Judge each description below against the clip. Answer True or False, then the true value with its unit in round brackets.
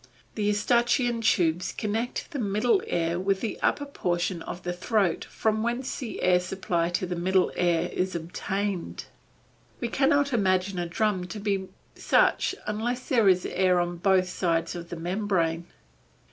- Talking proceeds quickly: False (160 wpm)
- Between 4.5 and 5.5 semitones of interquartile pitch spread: False (3.8 semitones)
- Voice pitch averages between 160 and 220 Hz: True (190 Hz)